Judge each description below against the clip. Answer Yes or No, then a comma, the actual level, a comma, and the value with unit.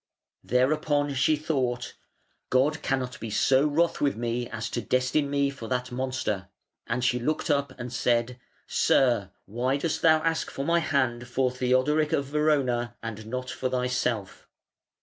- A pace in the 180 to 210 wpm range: No, average, 155 wpm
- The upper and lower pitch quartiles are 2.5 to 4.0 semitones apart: Yes, average, 2.9 semitones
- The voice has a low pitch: Yes, low, 130 Hz